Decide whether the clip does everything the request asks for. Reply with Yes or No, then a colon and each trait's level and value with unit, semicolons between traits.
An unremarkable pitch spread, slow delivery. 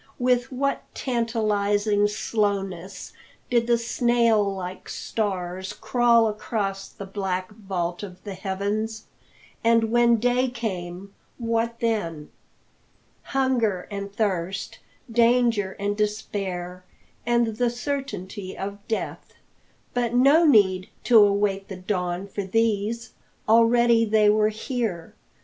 Yes: average, 3.2 semitones; slow, 110 wpm